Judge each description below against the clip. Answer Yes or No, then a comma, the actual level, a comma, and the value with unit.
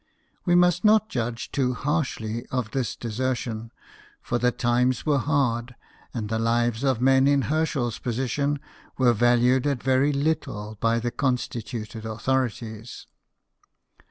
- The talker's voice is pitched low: Yes, low, 125 Hz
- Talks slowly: Yes, slow, 130 wpm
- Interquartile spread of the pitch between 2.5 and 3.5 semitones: Yes, average, 3.0 semitones